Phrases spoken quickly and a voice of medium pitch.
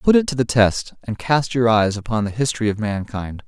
No: fast, 240 wpm; low, 115 Hz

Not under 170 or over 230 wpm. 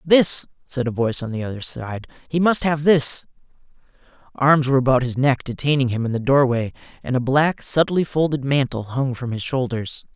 Yes: average, 190 wpm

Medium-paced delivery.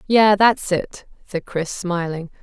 Yes: average, 150 wpm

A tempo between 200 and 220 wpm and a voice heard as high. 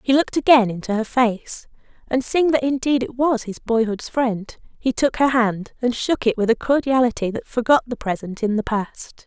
Yes: fast, 205 wpm; high, 240 Hz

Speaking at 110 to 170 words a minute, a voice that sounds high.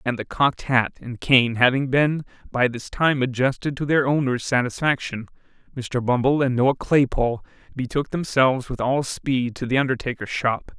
No: average, 165 wpm; low, 130 Hz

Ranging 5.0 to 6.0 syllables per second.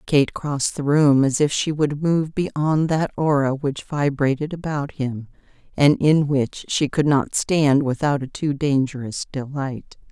No: 4.0 syllables/s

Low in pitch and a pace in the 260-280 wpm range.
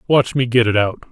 Yes: low, 120 Hz; fast, 270 wpm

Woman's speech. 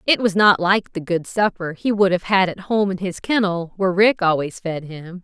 Yes: female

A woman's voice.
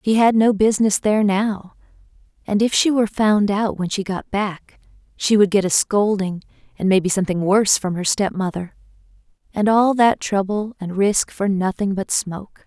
Yes: female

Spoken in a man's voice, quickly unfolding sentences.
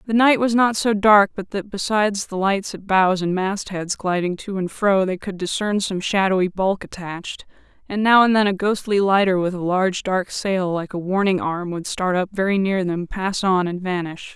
No: female; fast, 215 wpm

